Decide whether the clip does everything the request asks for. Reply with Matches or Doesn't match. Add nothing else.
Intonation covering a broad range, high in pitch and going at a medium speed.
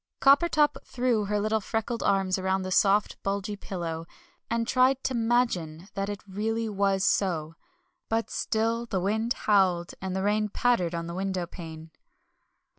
Doesn't match